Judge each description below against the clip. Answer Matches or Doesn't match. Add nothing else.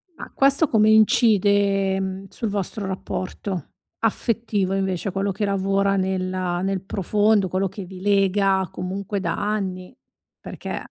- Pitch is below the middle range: Doesn't match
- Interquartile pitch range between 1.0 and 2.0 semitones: Matches